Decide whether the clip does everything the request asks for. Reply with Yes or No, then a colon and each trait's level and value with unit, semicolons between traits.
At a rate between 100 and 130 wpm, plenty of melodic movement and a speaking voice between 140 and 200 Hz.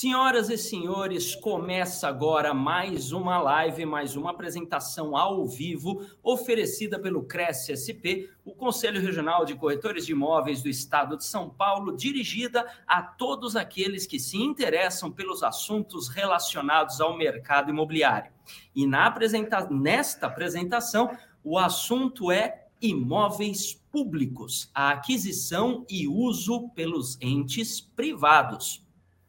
Yes: slow, 120 wpm; wide, 6.4 semitones; medium, 185 Hz